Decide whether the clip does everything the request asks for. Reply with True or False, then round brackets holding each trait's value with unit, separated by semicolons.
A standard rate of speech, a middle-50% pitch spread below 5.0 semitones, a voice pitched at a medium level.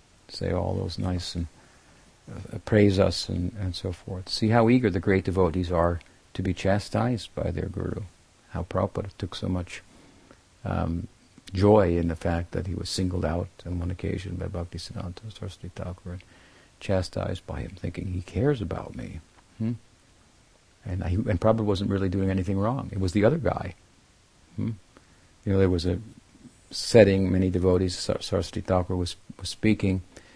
False (170 wpm; 2.4 semitones; 95 Hz)